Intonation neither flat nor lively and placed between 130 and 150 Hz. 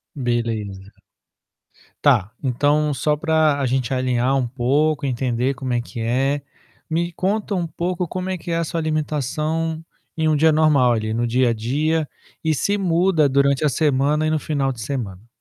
Yes: average, 4.3 semitones; medium, 140 Hz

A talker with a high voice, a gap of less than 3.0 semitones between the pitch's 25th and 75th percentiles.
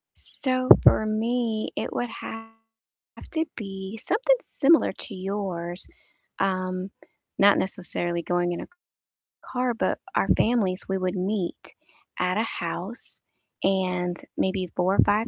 No: high, 195 Hz; average, 3.6 semitones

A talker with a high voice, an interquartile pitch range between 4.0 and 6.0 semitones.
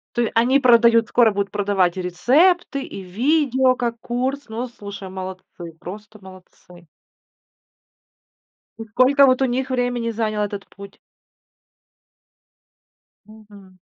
Yes: high, 225 Hz; average, 4.4 semitones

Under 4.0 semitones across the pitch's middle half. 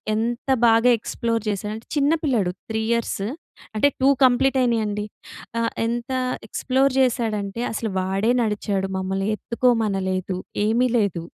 Yes: average, 3.1 semitones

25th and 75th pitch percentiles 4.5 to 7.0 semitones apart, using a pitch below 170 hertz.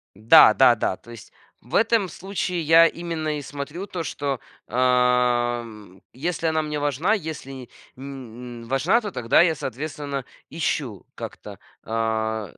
Yes: average, 5.2 semitones; low, 135 Hz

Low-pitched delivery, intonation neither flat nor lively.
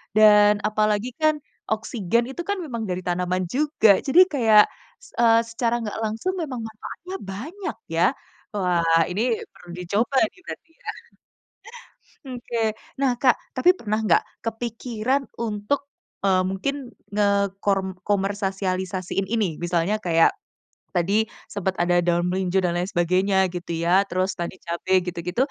No: high, 205 Hz; average, 4.1 semitones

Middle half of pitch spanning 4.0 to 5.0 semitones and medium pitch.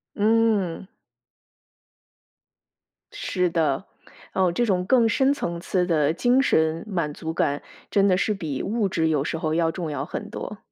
Yes: average, 4.5 semitones; medium, 175 Hz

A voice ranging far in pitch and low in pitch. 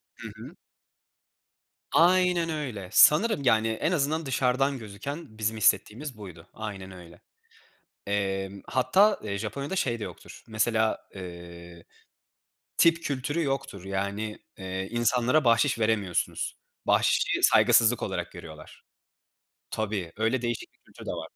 Yes: wide, 5.9 semitones; low, 110 Hz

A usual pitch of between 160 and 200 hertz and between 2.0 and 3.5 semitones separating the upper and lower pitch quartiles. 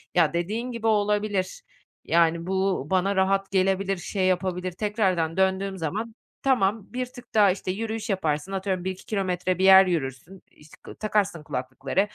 Yes: high, 190 Hz; narrow, 2.5 semitones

